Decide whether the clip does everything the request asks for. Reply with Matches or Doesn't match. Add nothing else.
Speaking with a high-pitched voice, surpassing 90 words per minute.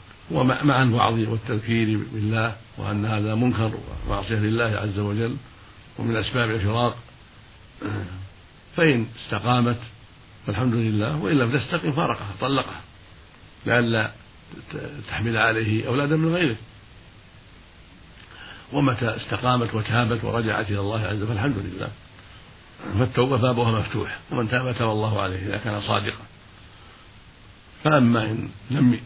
Doesn't match